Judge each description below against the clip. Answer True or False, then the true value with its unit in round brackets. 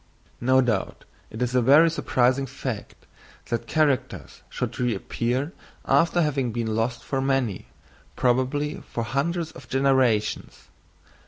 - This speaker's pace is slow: True (120 wpm)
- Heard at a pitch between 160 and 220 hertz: False (130 Hz)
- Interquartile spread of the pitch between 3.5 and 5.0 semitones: False (2.8 semitones)